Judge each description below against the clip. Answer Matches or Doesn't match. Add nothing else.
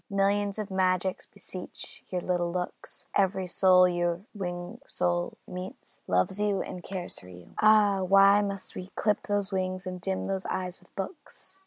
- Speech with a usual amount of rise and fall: Doesn't match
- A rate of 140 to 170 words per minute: Matches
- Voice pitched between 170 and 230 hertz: Matches